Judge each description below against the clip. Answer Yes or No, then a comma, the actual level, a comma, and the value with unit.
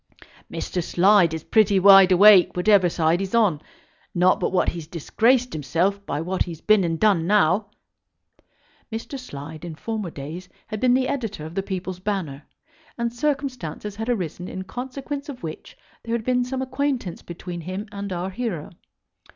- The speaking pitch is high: Yes, high, 195 Hz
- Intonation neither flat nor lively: Yes, average, 5.0 semitones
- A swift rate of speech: No, average, 165 wpm